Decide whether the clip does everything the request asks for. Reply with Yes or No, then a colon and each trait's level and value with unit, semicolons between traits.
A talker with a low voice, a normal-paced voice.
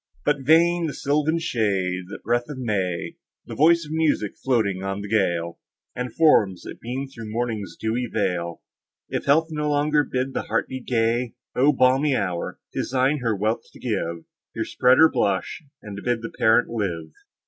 Yes: low, 120 Hz; average, 175 wpm